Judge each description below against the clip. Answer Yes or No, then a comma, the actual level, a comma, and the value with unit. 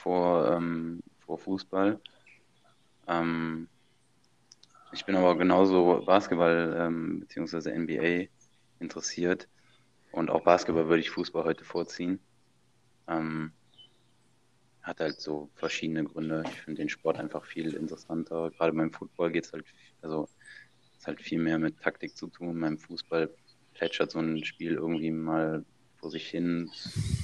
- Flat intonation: Yes, narrow, 1.8 semitones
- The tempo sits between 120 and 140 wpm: Yes, average, 135 wpm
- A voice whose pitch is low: Yes, very low, 85 Hz